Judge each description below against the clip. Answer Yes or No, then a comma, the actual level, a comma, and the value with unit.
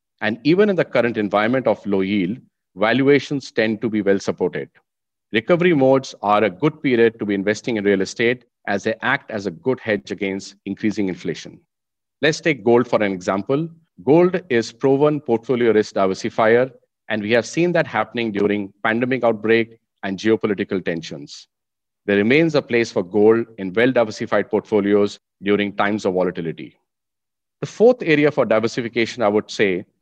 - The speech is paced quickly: No, average, 165 wpm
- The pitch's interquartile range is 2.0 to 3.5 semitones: No, average, 4.0 semitones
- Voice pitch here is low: Yes, low, 110 Hz